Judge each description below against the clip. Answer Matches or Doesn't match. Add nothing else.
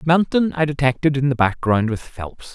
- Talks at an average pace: Matches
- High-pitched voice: Doesn't match